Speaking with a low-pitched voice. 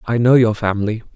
Yes: low, 110 Hz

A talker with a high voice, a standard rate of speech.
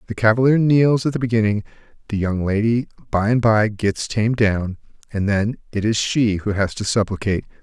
No: low, 110 Hz; average, 190 wpm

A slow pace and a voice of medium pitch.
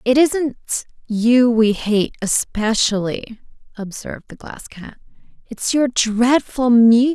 No: slow, 120 wpm; high, 235 Hz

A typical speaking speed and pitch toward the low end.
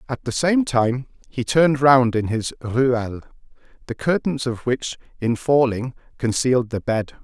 Yes: average, 160 wpm; low, 125 Hz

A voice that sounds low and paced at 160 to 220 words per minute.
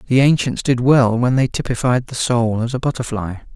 Yes: low, 125 Hz; average, 200 wpm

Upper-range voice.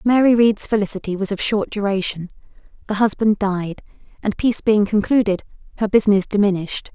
Yes: high, 205 Hz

